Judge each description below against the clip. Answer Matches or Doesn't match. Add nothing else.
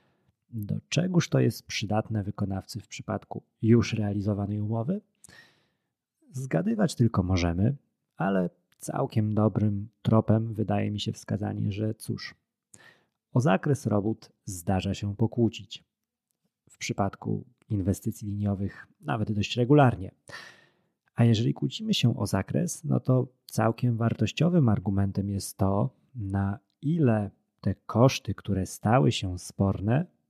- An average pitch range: Matches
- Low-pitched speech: Matches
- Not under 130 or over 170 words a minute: Doesn't match